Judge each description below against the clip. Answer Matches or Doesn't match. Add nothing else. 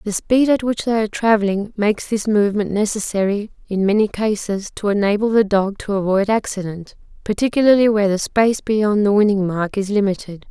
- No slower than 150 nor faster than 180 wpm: Matches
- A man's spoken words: Doesn't match